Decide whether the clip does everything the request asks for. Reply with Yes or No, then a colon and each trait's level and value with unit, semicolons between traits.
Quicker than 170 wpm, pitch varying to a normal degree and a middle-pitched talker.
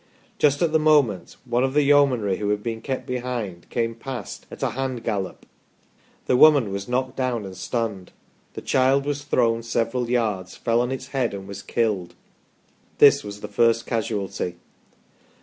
No: average, 180 wpm; average, 4.2 semitones; low, 115 Hz